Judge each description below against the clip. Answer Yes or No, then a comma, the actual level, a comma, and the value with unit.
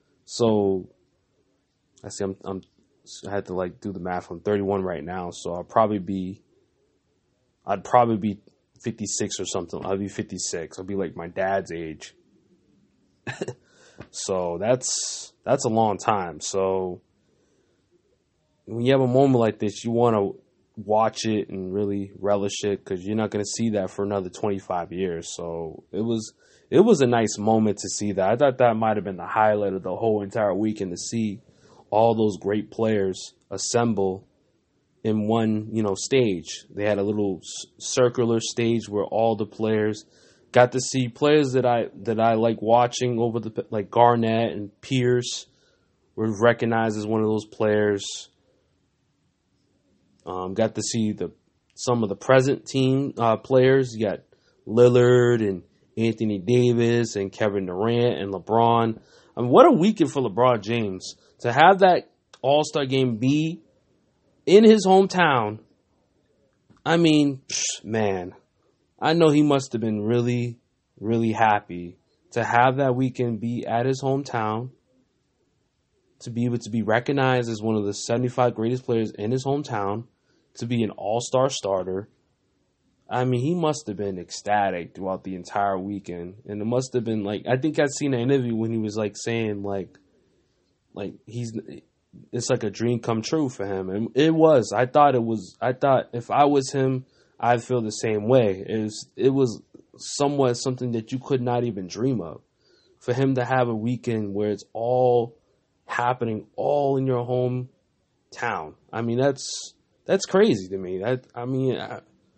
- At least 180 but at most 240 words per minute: No, average, 170 wpm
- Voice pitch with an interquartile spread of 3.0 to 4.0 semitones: Yes, average, 3.6 semitones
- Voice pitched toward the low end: Yes, low, 115 Hz